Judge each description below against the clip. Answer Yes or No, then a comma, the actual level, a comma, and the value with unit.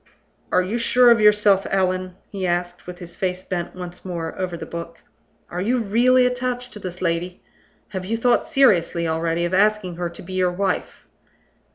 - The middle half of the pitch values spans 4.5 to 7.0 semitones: No, average, 3.2 semitones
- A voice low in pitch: No, medium, 185 Hz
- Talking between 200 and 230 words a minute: No, average, 185 wpm